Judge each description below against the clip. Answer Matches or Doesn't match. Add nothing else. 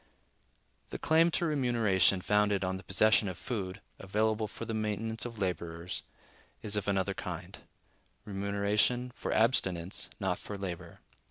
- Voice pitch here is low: Matches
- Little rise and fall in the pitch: Doesn't match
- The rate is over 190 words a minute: Doesn't match